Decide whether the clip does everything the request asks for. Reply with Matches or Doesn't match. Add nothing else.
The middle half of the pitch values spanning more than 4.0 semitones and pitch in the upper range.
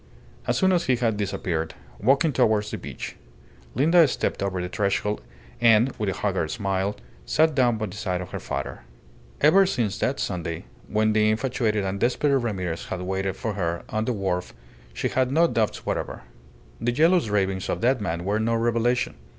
Doesn't match